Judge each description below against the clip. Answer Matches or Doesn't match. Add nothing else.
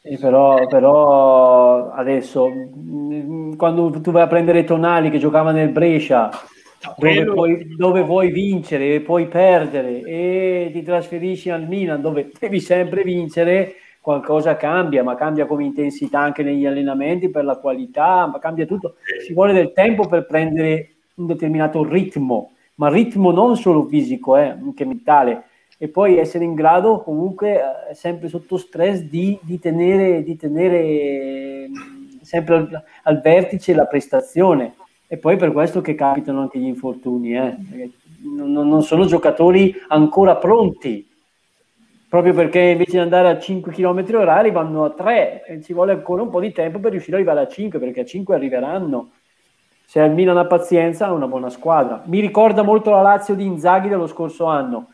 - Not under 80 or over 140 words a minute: Doesn't match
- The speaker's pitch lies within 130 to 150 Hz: Doesn't match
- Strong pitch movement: Doesn't match